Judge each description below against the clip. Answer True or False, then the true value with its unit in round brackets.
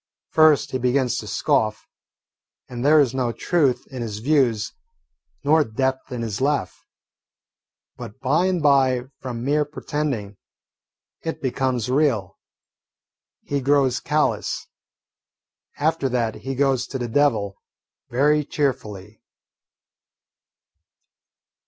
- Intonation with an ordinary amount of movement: True (3.6 semitones)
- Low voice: True (130 Hz)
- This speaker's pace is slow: True (110 wpm)